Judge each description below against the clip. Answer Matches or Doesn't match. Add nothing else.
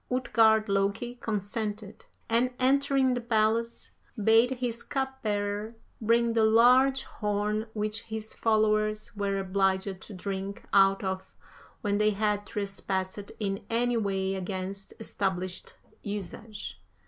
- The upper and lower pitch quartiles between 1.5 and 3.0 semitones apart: Matches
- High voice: Matches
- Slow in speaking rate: Matches